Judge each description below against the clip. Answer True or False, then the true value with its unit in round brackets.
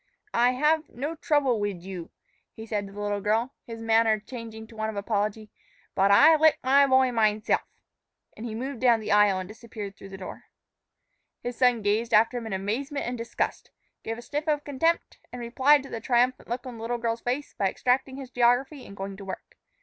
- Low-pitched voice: False (230 Hz)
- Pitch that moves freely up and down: False (3.6 semitones)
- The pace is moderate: False (210 wpm)